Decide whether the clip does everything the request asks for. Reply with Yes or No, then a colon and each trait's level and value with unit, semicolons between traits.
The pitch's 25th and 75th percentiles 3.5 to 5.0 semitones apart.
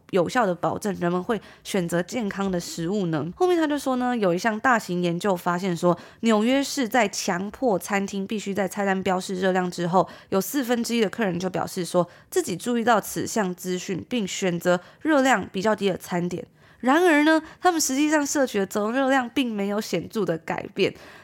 No: wide, 5.4 semitones